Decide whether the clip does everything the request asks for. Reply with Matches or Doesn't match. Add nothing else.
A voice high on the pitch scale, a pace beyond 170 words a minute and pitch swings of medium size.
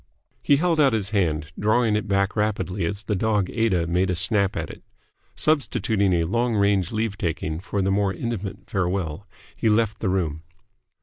Doesn't match